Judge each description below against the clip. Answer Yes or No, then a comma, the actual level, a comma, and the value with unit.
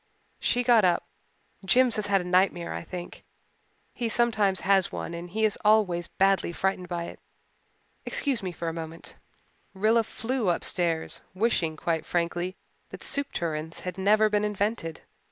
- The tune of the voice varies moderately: Yes, average, 3.9 semitones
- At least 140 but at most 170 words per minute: Yes, average, 155 wpm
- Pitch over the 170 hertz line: Yes, high, 190 Hz